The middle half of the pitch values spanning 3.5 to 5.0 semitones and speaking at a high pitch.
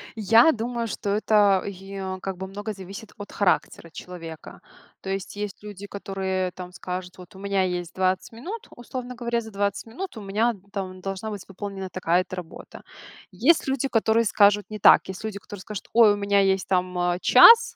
No: average, 2.9 semitones; high, 200 Hz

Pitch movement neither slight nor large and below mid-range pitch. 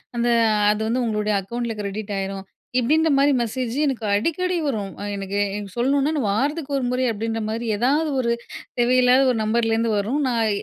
No: average, 3.8 semitones; high, 235 Hz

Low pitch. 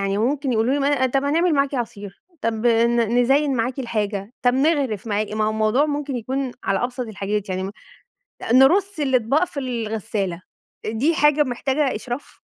No: high, 245 Hz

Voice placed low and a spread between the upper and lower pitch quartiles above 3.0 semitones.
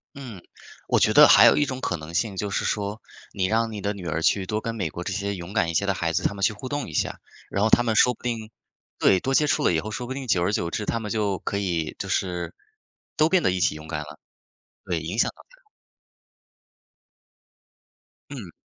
Yes: low, 100 Hz; average, 4.5 semitones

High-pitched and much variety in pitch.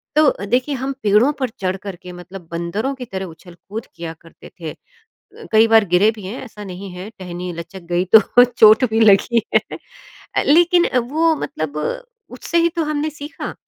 Yes: high, 215 Hz; wide, 7.0 semitones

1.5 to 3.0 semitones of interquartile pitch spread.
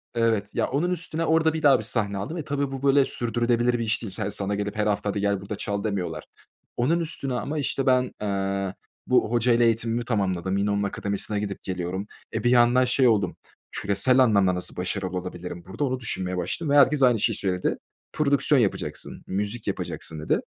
No: average, 4.5 semitones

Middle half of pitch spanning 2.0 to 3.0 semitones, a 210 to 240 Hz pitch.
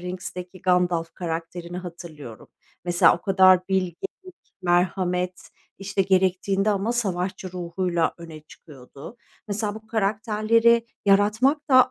No: average, 2.7 semitones; medium, 185 Hz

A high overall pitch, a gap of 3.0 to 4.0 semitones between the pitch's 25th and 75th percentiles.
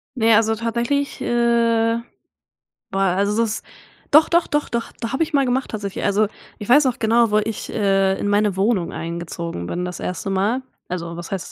Yes: high, 215 Hz; average, 3.5 semitones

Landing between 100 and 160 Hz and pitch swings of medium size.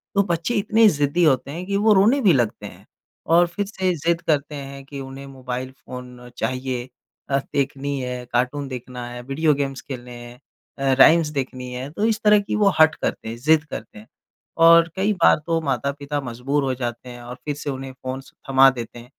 Yes: medium, 140 Hz; average, 4.6 semitones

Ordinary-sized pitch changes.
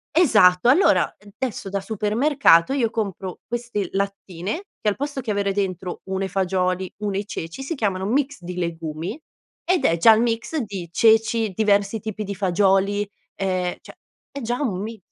Yes: average, 3.7 semitones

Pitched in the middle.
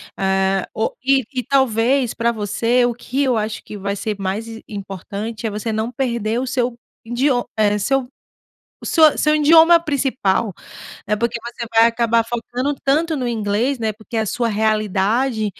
No: high, 230 Hz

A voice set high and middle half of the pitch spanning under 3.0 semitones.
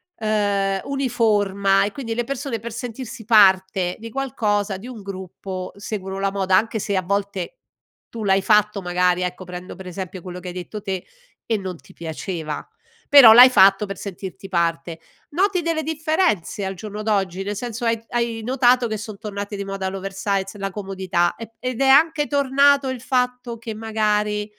No: high, 205 Hz; average, 3.5 semitones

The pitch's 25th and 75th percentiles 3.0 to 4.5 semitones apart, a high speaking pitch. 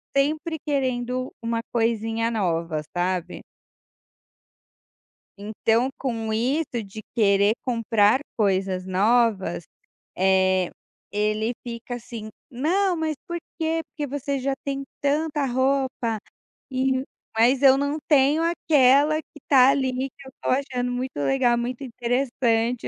Yes: average, 3.9 semitones; high, 245 Hz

